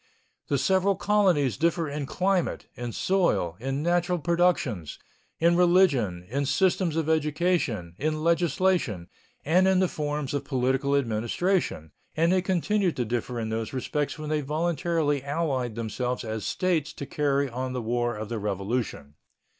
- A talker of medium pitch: Yes, medium, 145 Hz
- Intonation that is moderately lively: No, wide, 6.1 semitones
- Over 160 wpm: No, average, 150 wpm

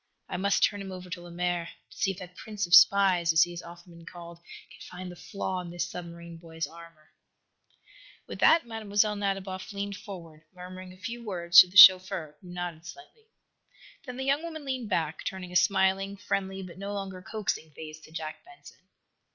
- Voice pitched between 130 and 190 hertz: Yes, medium, 185 Hz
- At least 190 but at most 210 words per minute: Yes, average, 195 wpm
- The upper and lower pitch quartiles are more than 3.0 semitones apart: No, average, 2.7 semitones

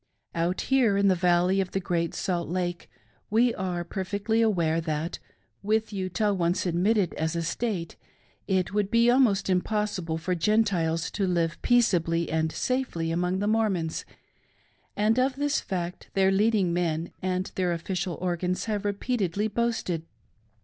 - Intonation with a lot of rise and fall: No, average, 3.7 semitones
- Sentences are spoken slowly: No, average, 150 wpm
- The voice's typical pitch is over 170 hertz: Yes, medium, 185 Hz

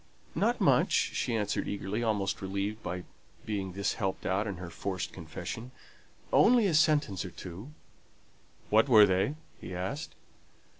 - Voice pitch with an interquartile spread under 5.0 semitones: Yes, average, 3.3 semitones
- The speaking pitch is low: Yes, low, 100 Hz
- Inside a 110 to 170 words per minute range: Yes, average, 145 wpm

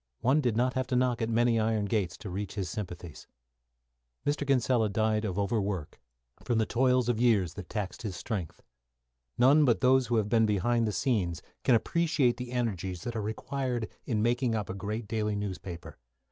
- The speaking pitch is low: Yes, low, 110 Hz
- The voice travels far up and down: No, average, 3.4 semitones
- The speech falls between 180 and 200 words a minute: Yes, average, 190 wpm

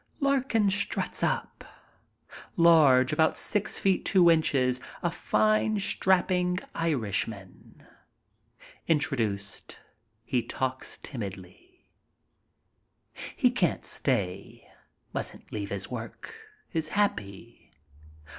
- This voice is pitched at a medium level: Yes, medium, 155 Hz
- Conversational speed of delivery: No, slow, 85 wpm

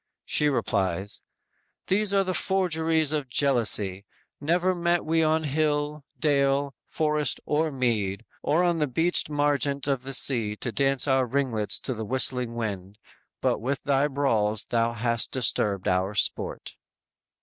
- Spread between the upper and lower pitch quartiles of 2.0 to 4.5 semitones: No, average, 5.0 semitones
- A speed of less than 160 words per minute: Yes, average, 145 wpm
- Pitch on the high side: No, low, 135 Hz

